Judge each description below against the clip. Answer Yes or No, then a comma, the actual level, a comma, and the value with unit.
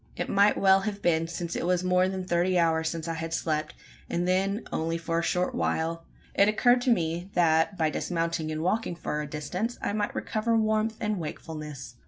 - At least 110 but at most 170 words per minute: No, fast, 205 wpm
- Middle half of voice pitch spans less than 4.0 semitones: Yes, average, 3.5 semitones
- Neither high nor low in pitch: Yes, medium, 175 Hz